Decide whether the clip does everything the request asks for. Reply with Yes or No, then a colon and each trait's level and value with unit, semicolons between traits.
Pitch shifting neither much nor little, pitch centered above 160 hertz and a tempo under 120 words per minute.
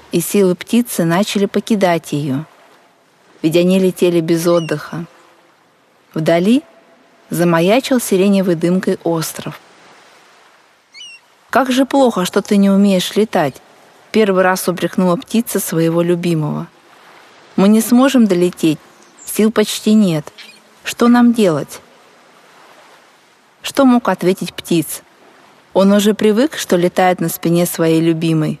Yes: average, 3.5 semitones; medium, 185 Hz; slow, 110 wpm